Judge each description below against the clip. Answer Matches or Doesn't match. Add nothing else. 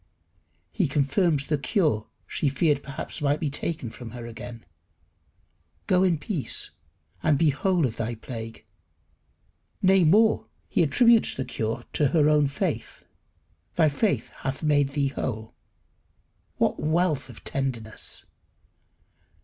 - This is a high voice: Doesn't match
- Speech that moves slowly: Matches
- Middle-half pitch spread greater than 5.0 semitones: Doesn't match